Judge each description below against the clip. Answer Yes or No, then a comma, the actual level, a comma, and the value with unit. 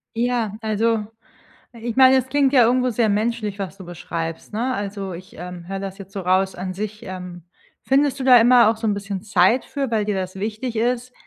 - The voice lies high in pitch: Yes, high, 215 Hz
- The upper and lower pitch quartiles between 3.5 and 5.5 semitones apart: Yes, average, 4.1 semitones